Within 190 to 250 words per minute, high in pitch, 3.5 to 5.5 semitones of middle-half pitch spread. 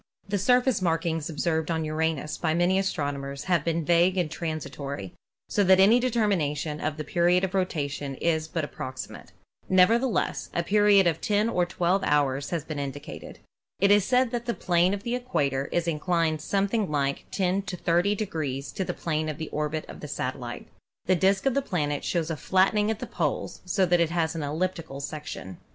No: average, 195 wpm; medium, 170 Hz; average, 4.2 semitones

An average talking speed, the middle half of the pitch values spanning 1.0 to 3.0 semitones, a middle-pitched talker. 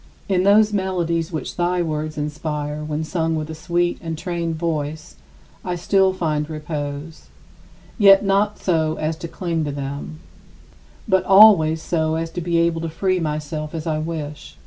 Yes: average, 165 wpm; narrow, 2.5 semitones; medium, 160 Hz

